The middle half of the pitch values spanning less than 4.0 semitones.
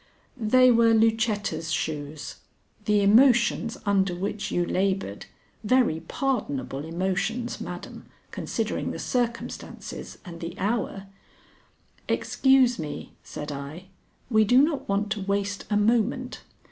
No: average, 5.1 semitones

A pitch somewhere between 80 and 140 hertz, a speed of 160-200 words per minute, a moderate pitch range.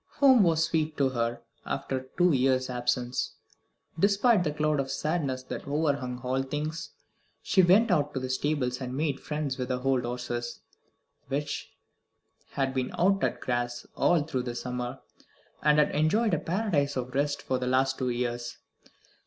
Yes: low, 135 Hz; average, 170 wpm; average, 3.7 semitones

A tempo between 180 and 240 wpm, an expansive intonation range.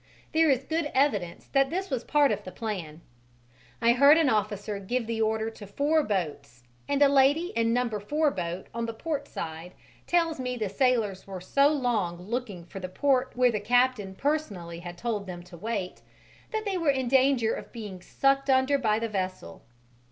Yes: average, 190 wpm; wide, 6.2 semitones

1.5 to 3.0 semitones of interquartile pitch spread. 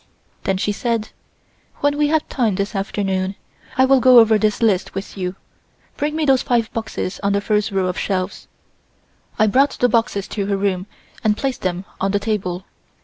No: average, 3.7 semitones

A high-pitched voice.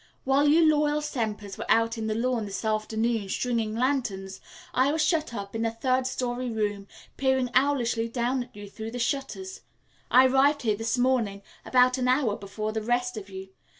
Yes: high, 240 Hz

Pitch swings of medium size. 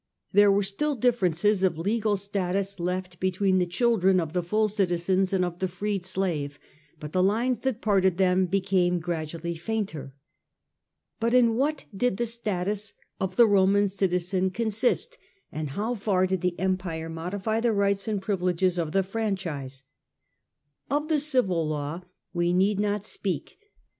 Yes: average, 3.0 semitones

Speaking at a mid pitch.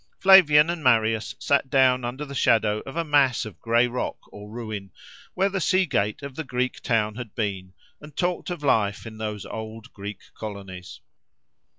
No: low, 120 Hz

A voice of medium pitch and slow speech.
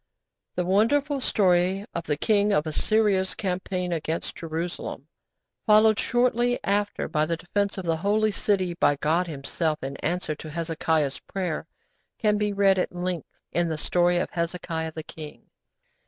No: medium, 180 Hz; average, 155 wpm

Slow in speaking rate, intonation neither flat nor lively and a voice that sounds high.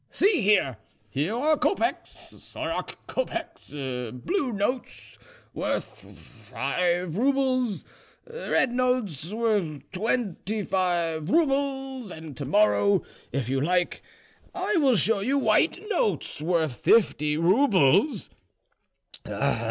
No: slow, 100 wpm; wide, 7.7 semitones; high, 210 Hz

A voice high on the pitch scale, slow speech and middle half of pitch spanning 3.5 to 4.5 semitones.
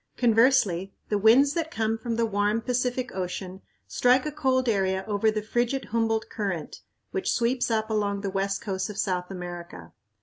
No: high, 220 Hz; average, 170 wpm; average, 3.9 semitones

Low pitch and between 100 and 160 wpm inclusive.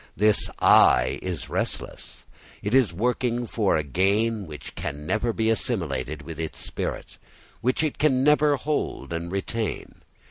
Yes: low, 105 Hz; average, 145 wpm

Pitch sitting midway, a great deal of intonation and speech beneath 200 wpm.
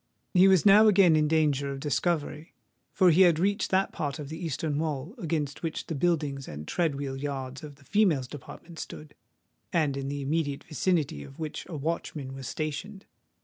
No: medium, 155 Hz; average, 3.6 semitones; average, 190 wpm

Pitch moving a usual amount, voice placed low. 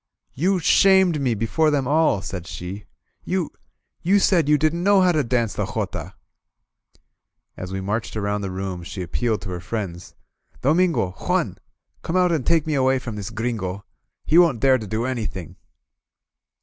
No: wide, 8.4 semitones; low, 125 Hz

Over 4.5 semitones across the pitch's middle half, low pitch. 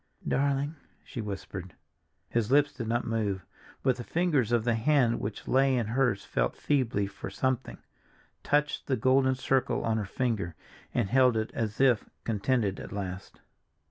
No: average, 3.9 semitones; low, 120 Hz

